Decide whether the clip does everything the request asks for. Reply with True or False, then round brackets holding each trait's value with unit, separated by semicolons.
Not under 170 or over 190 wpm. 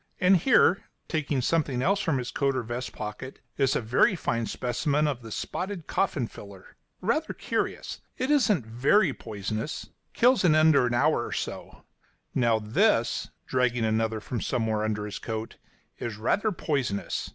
False (155 wpm)